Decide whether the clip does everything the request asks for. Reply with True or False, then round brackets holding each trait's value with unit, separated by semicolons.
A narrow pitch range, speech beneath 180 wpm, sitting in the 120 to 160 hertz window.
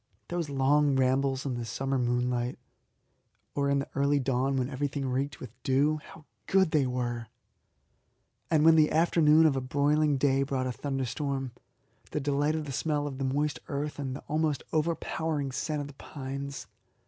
True (2.1 semitones; 170 wpm; 140 Hz)